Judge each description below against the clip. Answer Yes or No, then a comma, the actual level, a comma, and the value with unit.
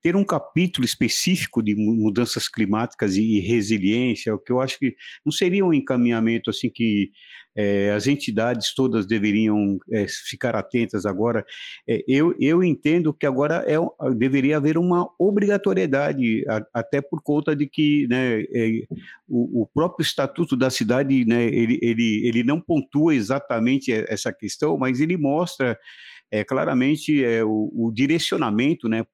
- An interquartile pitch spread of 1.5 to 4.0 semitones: No, average, 4.9 semitones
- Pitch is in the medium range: No, low, 125 Hz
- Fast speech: No, average, 150 wpm